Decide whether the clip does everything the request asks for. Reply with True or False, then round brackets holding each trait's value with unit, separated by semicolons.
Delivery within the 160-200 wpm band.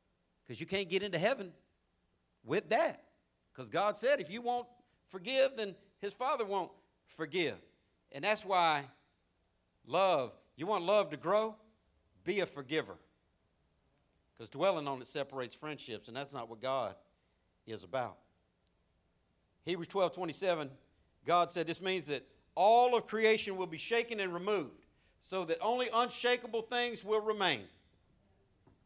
False (140 wpm)